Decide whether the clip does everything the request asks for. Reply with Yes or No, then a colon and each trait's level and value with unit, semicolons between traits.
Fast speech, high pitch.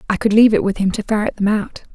Yes: fast, 310 wpm; high, 215 Hz